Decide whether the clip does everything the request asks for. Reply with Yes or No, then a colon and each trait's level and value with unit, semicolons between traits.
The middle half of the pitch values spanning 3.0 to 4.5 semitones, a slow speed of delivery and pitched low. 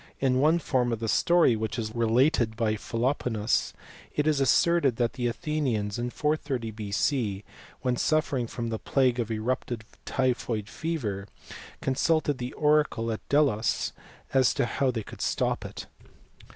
No: average, 4.0 semitones; average, 150 wpm; low, 125 Hz